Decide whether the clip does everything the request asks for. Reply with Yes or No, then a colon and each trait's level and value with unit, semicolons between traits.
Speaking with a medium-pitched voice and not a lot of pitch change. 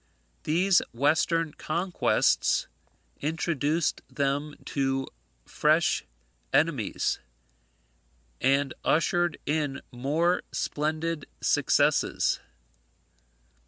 No: medium, 150 Hz; average, 3.0 semitones